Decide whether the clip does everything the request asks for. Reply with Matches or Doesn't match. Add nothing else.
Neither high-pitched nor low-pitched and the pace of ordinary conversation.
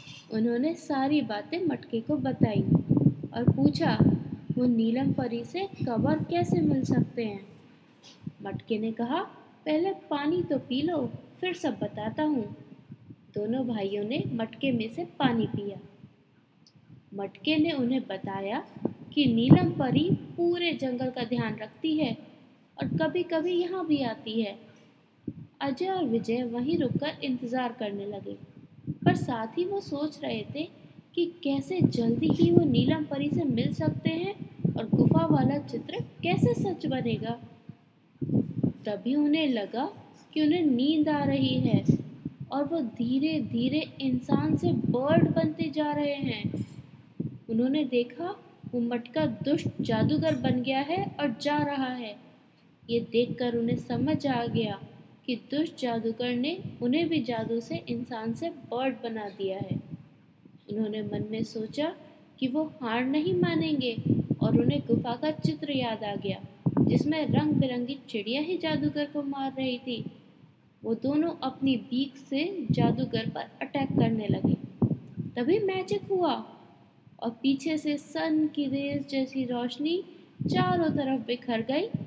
Doesn't match